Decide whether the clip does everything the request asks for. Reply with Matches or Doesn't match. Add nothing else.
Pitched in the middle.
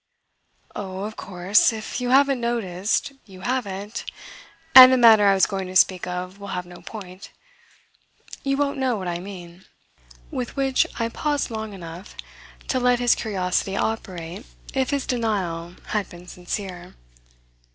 Doesn't match